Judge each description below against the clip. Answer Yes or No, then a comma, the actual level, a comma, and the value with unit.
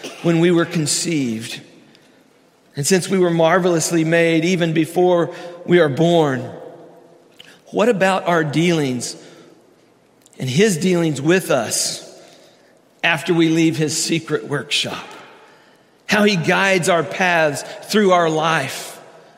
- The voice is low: No, medium, 165 Hz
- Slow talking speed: Yes, slow, 120 wpm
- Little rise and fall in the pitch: Yes, narrow, 1.7 semitones